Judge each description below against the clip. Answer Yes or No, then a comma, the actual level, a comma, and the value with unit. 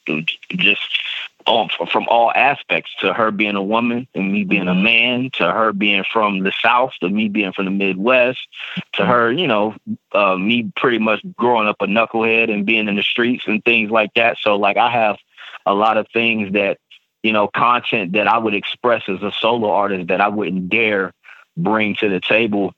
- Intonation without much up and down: Yes, narrow, 2.3 semitones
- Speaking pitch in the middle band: No, low, 110 Hz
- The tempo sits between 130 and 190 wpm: No, average, 200 wpm